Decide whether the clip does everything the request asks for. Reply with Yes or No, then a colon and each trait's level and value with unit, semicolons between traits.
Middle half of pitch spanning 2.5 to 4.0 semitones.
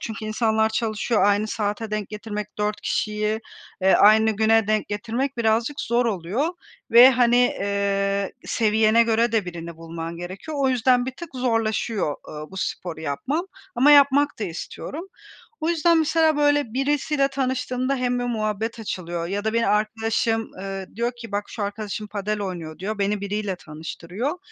Yes: average, 3.6 semitones